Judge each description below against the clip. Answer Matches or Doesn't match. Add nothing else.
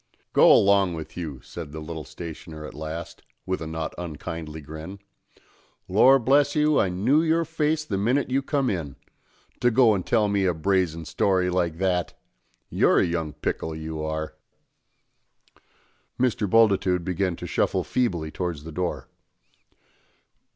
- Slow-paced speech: Doesn't match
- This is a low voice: Matches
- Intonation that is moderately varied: Doesn't match